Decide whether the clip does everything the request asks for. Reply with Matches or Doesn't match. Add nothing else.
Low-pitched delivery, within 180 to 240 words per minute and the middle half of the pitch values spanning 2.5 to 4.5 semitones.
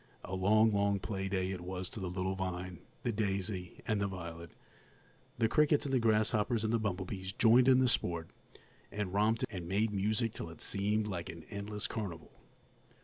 Matches